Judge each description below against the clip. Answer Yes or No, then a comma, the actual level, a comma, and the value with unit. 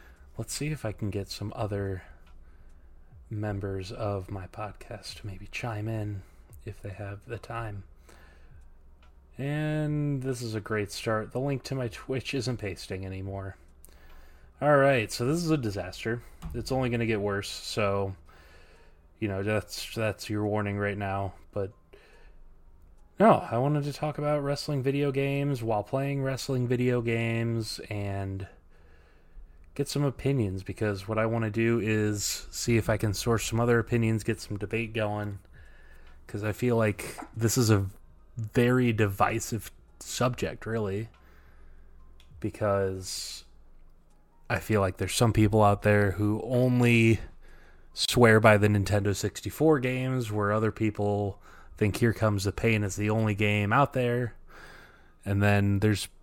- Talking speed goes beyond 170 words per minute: No, average, 150 wpm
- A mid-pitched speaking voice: No, low, 105 Hz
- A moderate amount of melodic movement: Yes, average, 4.1 semitones